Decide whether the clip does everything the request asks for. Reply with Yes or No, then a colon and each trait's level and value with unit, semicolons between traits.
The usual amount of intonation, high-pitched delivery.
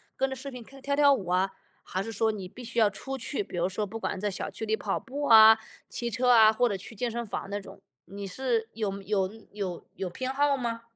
Yes: average, 4.0 semitones; high, 220 Hz